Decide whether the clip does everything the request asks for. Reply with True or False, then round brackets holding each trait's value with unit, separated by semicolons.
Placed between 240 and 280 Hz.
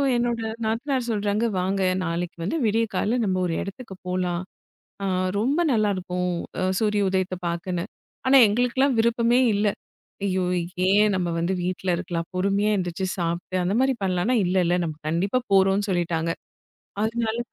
False (195 Hz)